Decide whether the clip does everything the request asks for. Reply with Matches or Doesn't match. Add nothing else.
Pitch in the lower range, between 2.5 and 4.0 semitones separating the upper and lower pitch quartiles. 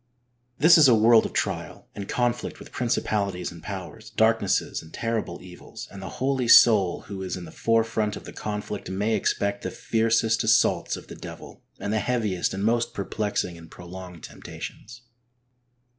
Matches